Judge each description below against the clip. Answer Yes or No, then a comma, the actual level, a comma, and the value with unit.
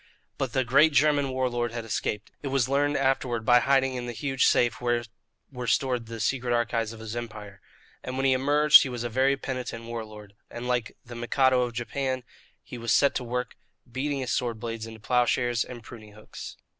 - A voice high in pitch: No, low, 125 Hz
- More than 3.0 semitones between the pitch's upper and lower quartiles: No, narrow, 2.4 semitones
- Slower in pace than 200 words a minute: No, fast, 205 wpm